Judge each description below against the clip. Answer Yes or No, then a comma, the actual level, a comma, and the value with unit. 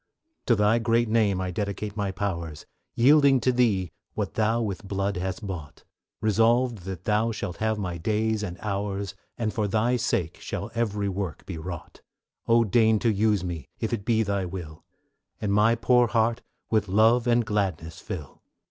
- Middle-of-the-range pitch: No, low, 105 Hz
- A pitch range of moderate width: Yes, average, 3.2 semitones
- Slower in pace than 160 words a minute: No, average, 175 wpm